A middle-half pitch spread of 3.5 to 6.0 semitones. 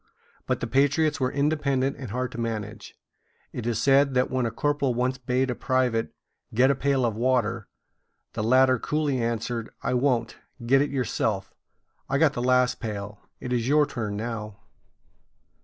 No: average, 2.8 semitones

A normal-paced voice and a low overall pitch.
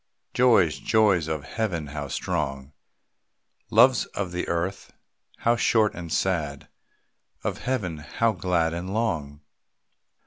No: slow, 115 wpm; very low, 85 Hz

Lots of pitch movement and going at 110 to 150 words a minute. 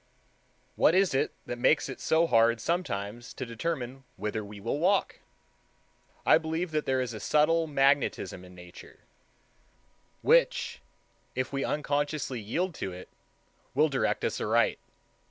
Yes: wide, 5.8 semitones; average, 140 wpm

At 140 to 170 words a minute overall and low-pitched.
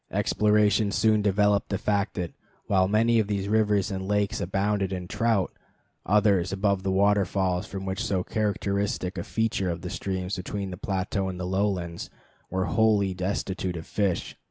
Yes: average, 165 wpm; low, 100 Hz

